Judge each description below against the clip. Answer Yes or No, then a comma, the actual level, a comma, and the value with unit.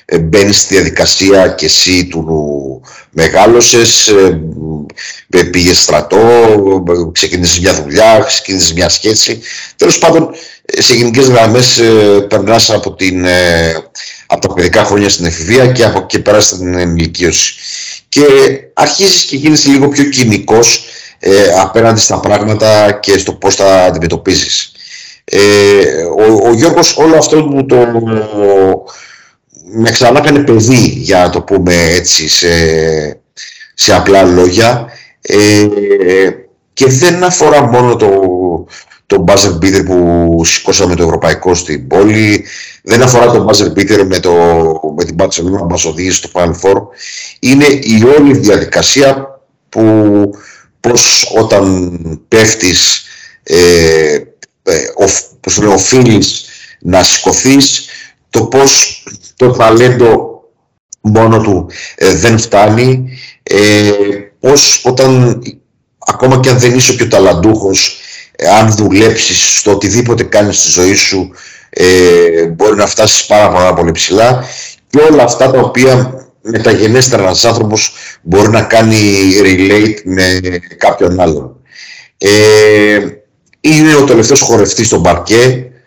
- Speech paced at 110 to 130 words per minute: Yes, average, 120 wpm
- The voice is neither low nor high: No, low, 105 Hz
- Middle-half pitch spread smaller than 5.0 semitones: No, average, 5.3 semitones